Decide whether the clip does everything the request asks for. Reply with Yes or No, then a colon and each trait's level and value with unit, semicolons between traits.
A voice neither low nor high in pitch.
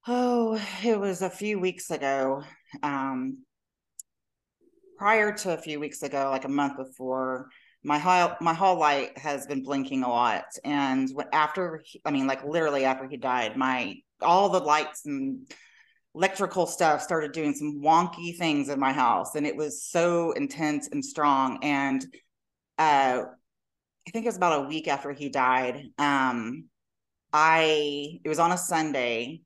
Yes: medium, 150 Hz